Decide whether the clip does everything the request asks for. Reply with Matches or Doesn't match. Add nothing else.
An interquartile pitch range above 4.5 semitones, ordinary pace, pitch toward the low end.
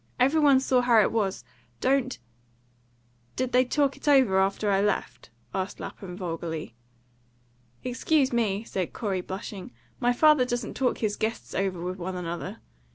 Doesn't match